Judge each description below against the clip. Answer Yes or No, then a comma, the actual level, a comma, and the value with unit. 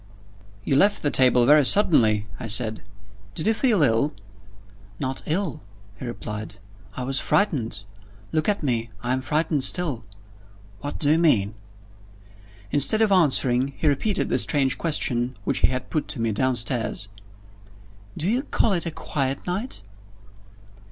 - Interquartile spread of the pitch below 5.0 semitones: No, wide, 5.5 semitones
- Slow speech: No, average, 145 wpm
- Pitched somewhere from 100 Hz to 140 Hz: Yes, low, 135 Hz